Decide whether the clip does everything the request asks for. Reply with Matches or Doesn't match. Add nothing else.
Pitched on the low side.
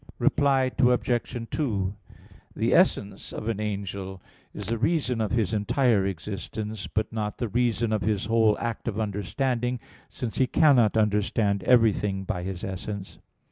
Matches